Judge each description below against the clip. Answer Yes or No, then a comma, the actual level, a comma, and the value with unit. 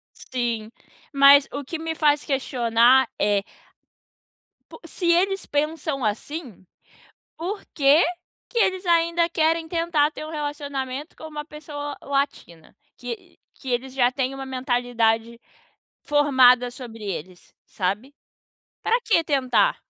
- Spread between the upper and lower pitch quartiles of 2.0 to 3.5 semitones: No, average, 4.3 semitones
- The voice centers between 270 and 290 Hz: Yes, very high, 275 Hz